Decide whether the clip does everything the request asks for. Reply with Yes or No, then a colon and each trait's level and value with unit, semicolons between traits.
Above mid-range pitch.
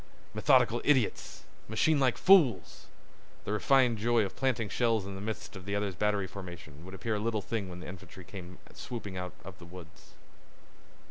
No: low, 105 Hz